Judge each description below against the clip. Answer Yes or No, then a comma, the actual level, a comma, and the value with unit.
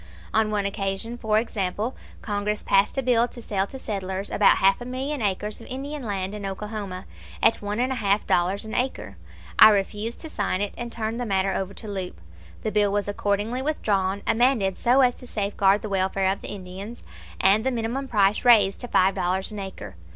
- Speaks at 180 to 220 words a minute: Yes, average, 200 wpm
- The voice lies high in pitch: Yes, high, 210 Hz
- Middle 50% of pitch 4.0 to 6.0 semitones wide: No, average, 3.2 semitones